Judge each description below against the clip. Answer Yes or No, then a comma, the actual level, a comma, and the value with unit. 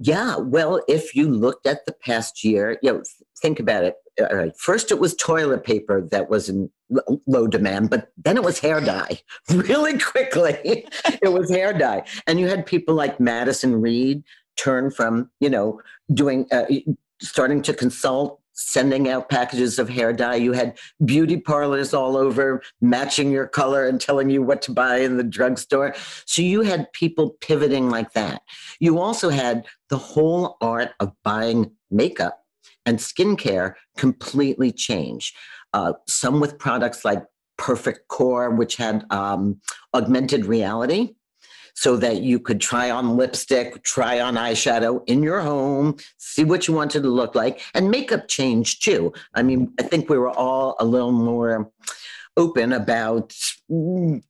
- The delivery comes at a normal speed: Yes, average, 160 wpm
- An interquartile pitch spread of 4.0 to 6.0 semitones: Yes, average, 4.3 semitones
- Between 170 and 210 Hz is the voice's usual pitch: No, low, 135 Hz